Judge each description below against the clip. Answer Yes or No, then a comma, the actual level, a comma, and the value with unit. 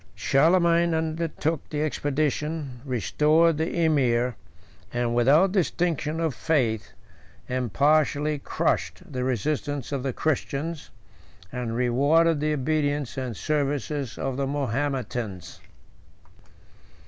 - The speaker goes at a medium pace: No, slow, 100 wpm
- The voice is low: No, medium, 145 Hz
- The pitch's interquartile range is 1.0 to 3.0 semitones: No, average, 3.7 semitones